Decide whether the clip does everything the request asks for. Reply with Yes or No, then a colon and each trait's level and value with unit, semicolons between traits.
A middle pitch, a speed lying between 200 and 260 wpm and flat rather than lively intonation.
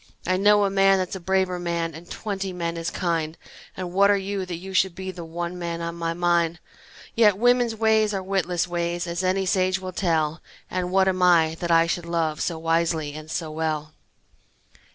Yes: medium, 175 Hz; fast, 205 wpm; narrow, 2.3 semitones